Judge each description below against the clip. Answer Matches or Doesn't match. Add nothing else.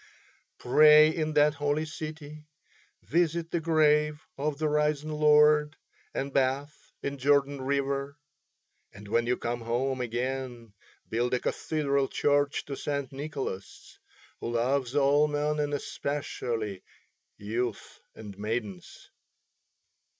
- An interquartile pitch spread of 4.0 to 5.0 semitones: Doesn't match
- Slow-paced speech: Matches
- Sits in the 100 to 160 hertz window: Matches